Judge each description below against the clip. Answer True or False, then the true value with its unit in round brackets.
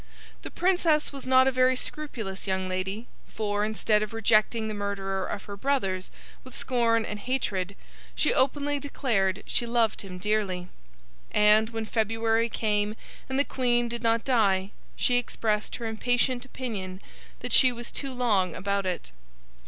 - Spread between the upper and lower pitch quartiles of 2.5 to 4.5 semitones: True (3.7 semitones)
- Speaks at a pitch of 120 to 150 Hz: False (220 Hz)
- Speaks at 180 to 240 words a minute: False (155 wpm)